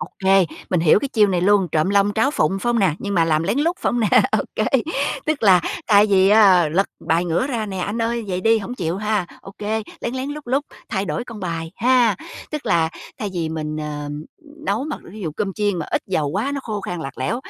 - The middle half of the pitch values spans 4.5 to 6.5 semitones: Yes, average, 4.8 semitones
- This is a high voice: Yes, high, 200 Hz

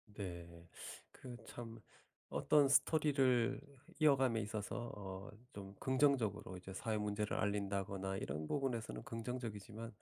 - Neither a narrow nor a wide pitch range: Yes, average, 4.3 semitones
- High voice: No, low, 110 Hz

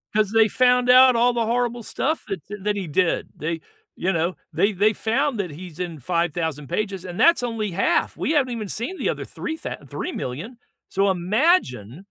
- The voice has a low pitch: No, high, 210 Hz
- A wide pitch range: Yes, wide, 5.8 semitones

